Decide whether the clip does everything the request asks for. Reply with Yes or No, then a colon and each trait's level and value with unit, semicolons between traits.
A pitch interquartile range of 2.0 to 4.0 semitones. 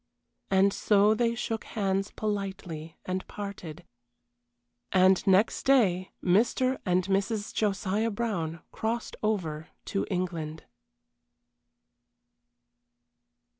Yes: average, 3.1 semitones